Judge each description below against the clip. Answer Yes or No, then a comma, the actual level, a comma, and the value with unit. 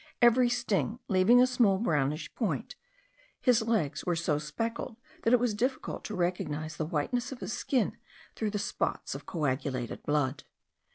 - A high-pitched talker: Yes, high, 200 Hz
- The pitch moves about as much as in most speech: No, wide, 7.8 semitones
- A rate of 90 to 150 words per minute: No, average, 165 wpm